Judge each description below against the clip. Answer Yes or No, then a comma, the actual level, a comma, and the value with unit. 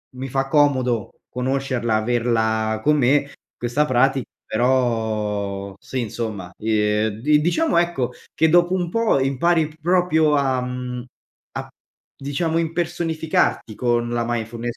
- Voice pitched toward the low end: Yes, low, 130 Hz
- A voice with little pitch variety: No, average, 4.9 semitones